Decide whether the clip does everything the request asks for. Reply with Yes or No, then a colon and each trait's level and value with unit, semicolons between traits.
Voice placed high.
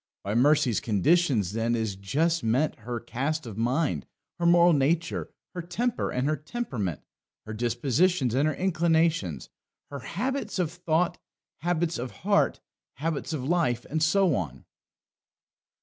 No: medium, 150 Hz